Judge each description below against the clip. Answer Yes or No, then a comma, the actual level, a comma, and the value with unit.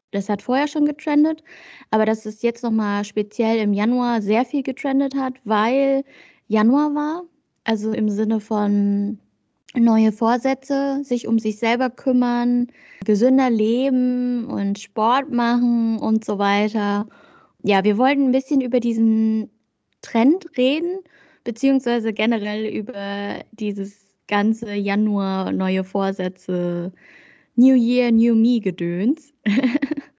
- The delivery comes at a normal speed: No, slow, 120 wpm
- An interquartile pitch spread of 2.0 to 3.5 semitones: No, average, 3.9 semitones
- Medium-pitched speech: No, high, 230 Hz